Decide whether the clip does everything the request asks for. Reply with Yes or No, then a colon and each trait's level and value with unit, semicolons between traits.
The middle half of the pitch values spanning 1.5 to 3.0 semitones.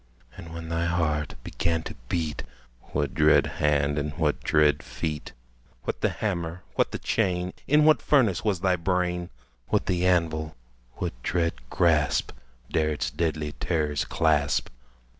Yes: average, 2.7 semitones